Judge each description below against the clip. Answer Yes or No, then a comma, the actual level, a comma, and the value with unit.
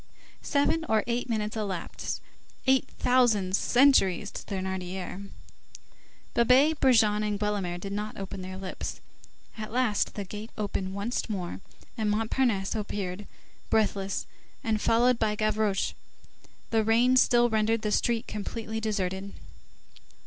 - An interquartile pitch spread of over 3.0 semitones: No, average, 2.7 semitones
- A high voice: Yes, high, 215 Hz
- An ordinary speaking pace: No, slow, 125 wpm